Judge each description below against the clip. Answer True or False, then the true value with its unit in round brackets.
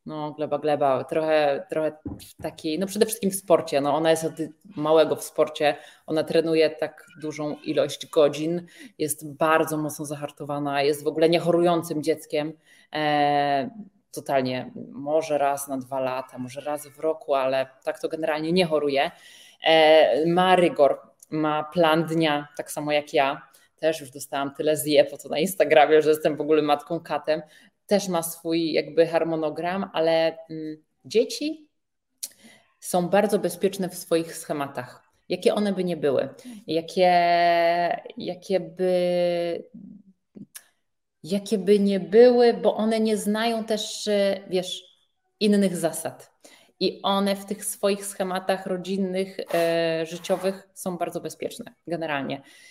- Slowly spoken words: False (135 wpm)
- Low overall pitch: False (160 Hz)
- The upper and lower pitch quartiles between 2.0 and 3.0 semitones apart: False (3.6 semitones)